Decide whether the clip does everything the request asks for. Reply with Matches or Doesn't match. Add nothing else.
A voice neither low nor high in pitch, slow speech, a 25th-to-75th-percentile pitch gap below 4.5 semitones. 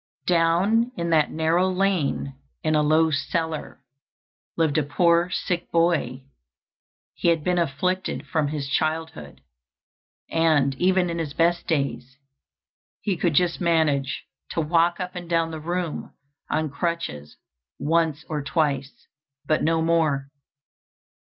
Matches